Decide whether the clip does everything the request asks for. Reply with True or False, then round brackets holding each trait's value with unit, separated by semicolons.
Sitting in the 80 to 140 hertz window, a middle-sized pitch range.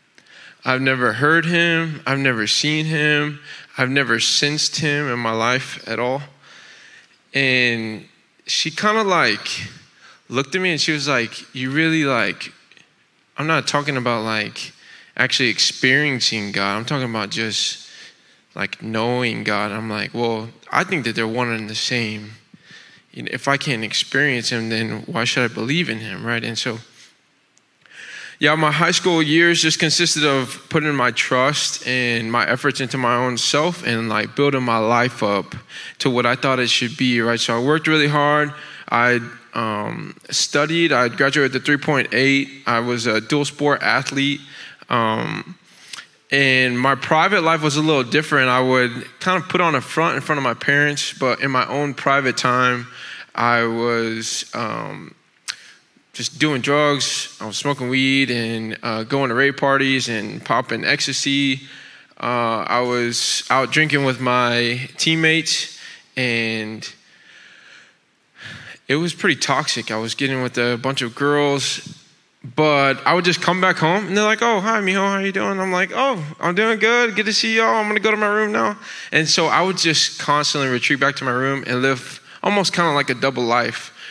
True (135 Hz; 4.1 semitones)